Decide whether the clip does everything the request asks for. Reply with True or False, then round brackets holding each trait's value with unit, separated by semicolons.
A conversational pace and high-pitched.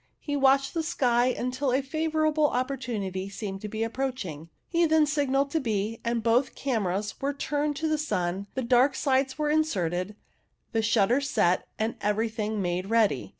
True (165 wpm; 245 Hz)